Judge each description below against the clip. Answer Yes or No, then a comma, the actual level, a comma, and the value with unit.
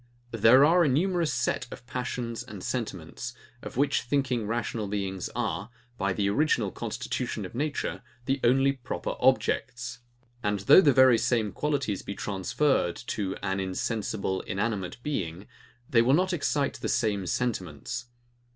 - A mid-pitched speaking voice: No, low, 120 Hz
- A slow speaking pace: No, average, 145 wpm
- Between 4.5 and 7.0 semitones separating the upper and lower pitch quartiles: Yes, average, 5.0 semitones